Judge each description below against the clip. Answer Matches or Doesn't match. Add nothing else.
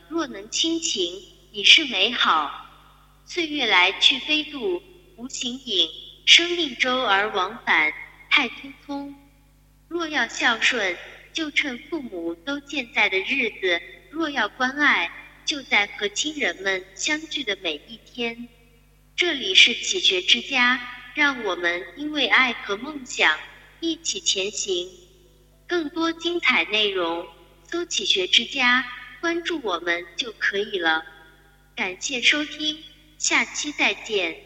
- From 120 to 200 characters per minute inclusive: Matches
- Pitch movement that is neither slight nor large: Doesn't match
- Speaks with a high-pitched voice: Matches